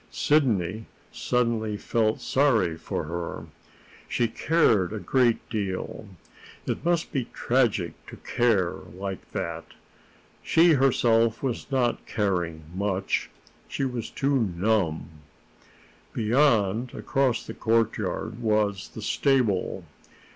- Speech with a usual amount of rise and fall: Yes, average, 4.5 semitones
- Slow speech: Yes, slow, 105 wpm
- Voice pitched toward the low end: Yes, low, 110 Hz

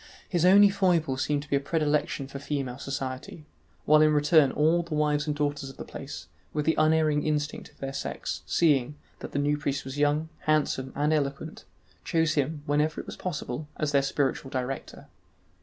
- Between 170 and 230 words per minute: Yes, average, 190 wpm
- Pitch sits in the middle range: Yes, medium, 150 Hz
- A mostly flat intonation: Yes, narrow, 2.0 semitones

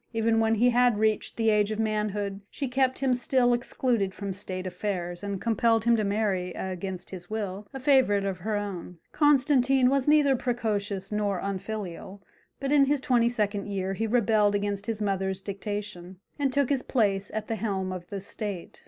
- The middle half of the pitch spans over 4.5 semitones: No, average, 3.7 semitones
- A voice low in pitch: No, high, 210 Hz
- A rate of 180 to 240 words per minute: Yes, average, 185 wpm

